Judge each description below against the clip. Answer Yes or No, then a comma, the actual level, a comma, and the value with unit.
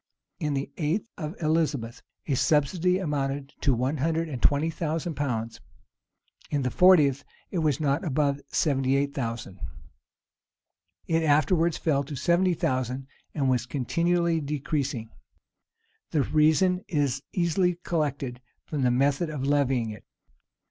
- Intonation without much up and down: No, average, 3.3 semitones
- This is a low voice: No, medium, 145 Hz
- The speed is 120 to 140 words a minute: Yes, slow, 135 wpm